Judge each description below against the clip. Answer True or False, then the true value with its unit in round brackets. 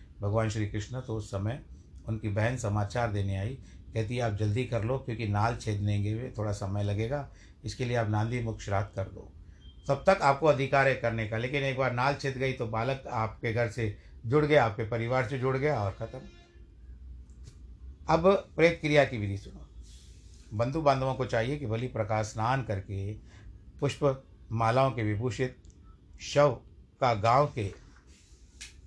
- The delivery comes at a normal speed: True (170 wpm)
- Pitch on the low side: True (110 Hz)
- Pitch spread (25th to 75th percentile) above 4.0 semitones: True (4.7 semitones)